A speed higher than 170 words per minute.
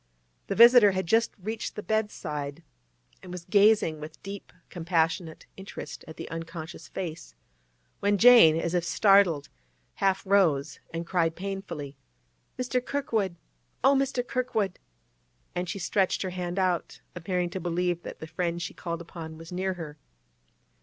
No: average, 145 wpm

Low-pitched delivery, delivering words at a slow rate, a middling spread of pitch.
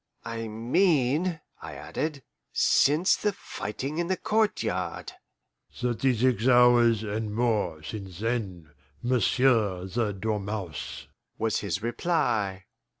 Yes: low, 115 Hz; slow, 105 wpm; average, 4.2 semitones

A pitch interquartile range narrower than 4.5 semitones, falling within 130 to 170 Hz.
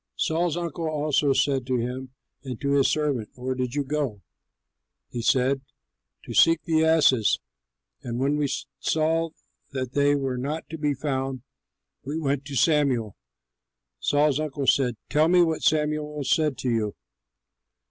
Yes: average, 2.8 semitones; medium, 140 Hz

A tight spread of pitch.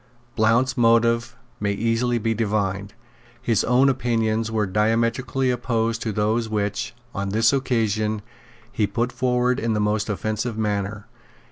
Yes: narrow, 2.1 semitones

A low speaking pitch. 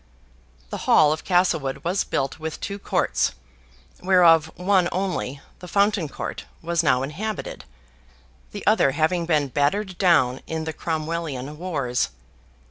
No: medium, 165 Hz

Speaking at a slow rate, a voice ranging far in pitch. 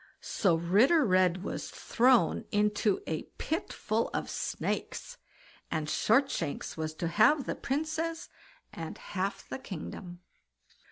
Yes: slow, 120 wpm; wide, 7.6 semitones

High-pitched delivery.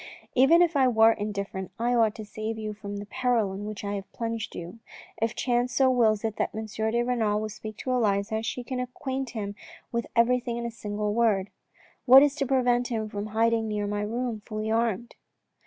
Yes: high, 225 Hz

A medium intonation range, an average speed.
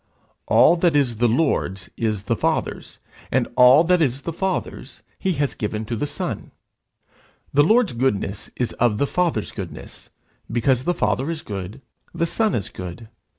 No: wide, 7.0 semitones; average, 165 wpm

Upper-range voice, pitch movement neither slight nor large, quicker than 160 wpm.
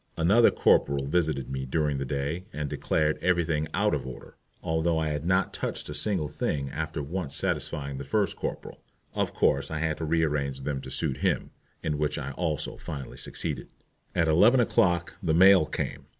No: very low, 75 Hz; average, 3.3 semitones; average, 180 wpm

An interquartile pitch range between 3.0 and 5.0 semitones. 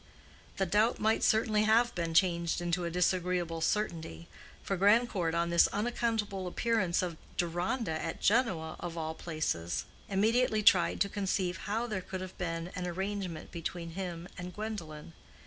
Yes: average, 3.8 semitones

